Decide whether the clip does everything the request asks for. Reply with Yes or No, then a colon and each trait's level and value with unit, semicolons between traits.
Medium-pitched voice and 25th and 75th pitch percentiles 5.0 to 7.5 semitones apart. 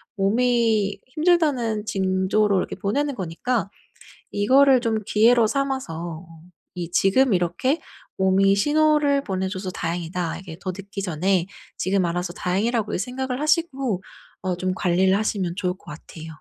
No: high, 200 Hz; average, 5.3 semitones